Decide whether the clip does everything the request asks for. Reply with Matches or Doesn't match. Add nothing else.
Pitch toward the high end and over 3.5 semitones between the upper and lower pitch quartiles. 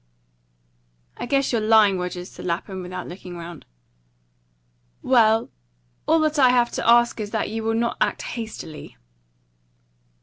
Matches